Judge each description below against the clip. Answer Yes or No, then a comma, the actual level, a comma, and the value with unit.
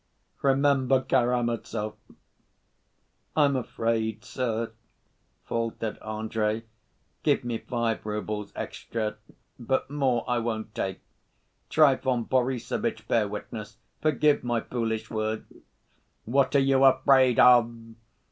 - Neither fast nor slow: No, slow, 100 wpm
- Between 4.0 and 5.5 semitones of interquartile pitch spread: No, average, 2.9 semitones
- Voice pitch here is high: No, low, 120 Hz